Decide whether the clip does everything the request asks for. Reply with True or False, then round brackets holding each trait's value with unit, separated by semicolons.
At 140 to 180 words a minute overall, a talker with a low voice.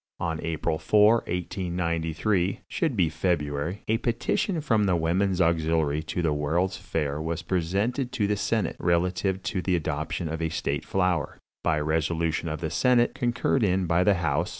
True (165 wpm; 85 Hz)